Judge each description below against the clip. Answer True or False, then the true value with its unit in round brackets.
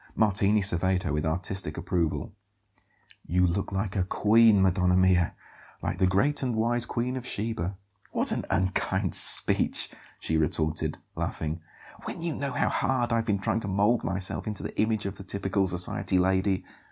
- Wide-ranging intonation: False (3.4 semitones)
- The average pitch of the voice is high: False (95 Hz)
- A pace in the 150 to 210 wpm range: True (165 wpm)